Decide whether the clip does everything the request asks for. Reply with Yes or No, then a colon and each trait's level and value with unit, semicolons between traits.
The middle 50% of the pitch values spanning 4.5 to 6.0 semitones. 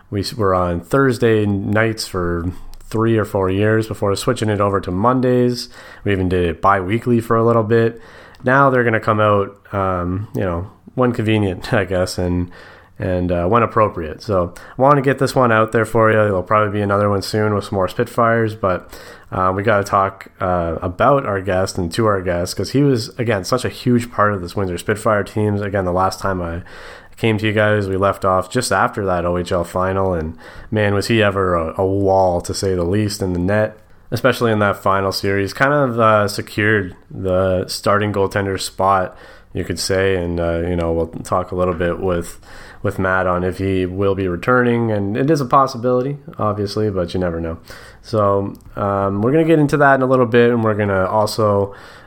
No: average, 3.3 semitones